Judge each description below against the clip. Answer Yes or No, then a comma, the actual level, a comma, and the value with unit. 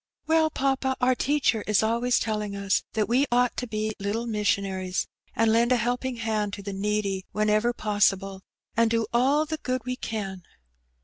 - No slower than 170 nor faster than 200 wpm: Yes, average, 175 wpm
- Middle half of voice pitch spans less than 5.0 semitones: Yes, average, 3.3 semitones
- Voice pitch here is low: No, high, 225 Hz